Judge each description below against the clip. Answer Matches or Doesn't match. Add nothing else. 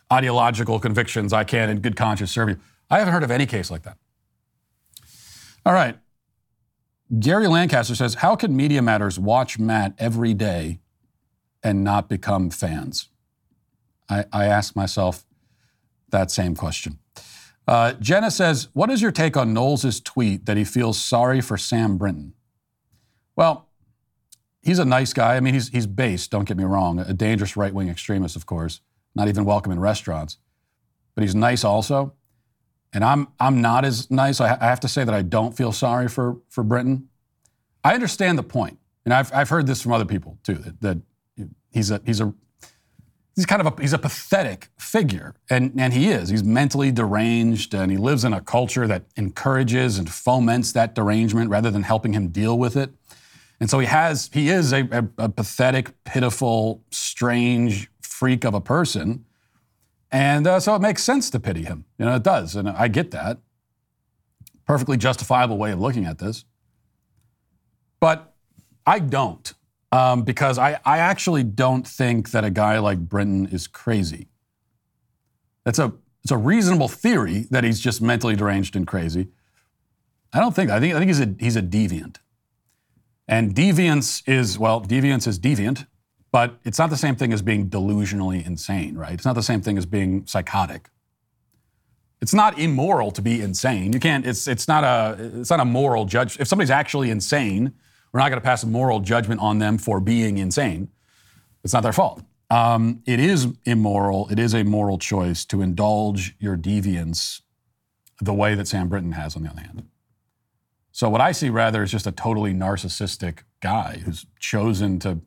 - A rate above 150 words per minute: Matches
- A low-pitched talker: Matches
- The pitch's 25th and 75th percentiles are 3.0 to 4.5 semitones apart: Matches